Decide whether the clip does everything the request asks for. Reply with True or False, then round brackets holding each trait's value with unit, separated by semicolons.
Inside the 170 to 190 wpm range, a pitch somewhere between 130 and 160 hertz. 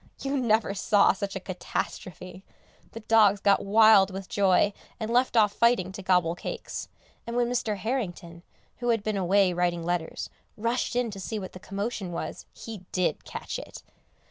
False (175 wpm; 200 Hz)